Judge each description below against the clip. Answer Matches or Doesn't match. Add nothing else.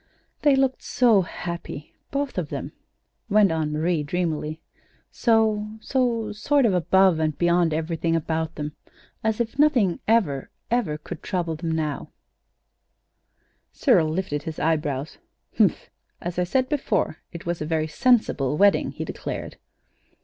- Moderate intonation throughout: Doesn't match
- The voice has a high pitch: Doesn't match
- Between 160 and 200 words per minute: Doesn't match